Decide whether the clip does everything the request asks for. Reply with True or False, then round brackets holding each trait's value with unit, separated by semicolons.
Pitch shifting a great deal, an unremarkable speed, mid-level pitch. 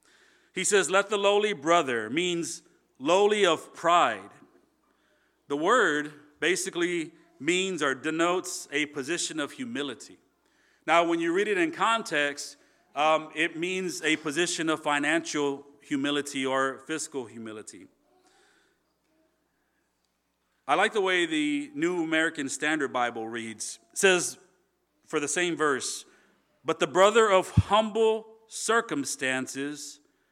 False (6.4 semitones; 120 wpm; 170 Hz)